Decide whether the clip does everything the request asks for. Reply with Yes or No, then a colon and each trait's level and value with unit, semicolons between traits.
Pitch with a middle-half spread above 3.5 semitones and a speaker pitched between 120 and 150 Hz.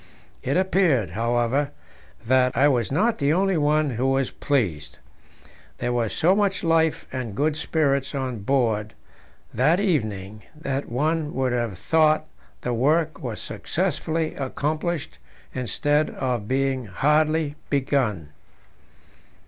Yes: average, 4.4 semitones; low, 135 Hz